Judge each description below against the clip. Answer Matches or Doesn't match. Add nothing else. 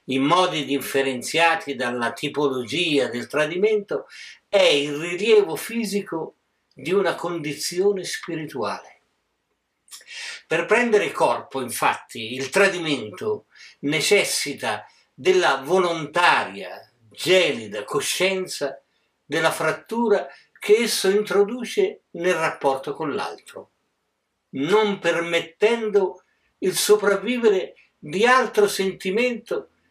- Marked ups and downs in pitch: Matches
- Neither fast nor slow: Doesn't match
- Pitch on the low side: Doesn't match